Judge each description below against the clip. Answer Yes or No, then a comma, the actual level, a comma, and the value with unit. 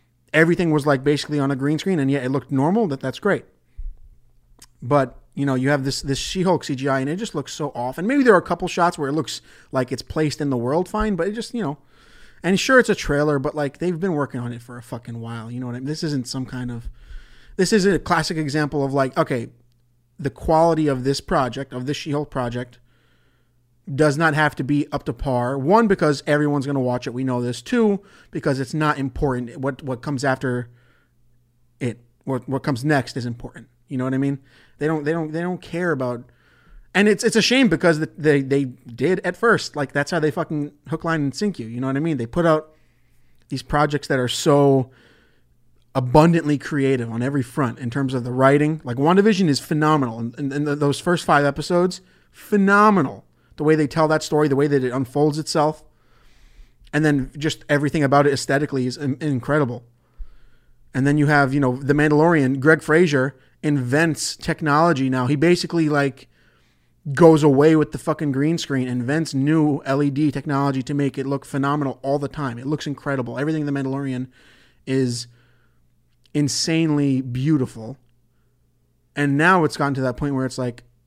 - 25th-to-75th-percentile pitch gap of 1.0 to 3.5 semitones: Yes, average, 3.2 semitones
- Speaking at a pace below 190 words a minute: No, fast, 205 wpm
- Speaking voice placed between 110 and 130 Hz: No, medium, 140 Hz